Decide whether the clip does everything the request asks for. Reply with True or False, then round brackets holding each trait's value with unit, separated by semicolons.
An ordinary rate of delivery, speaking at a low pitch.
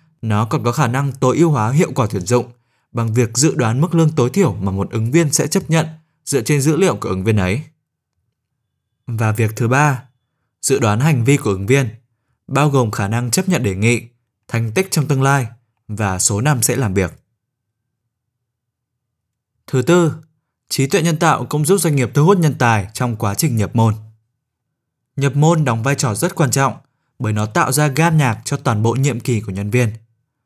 True (210 wpm; 125 Hz)